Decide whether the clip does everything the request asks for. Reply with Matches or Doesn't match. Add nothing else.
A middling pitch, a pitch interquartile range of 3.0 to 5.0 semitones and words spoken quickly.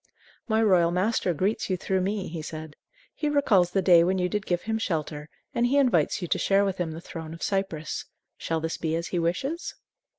Matches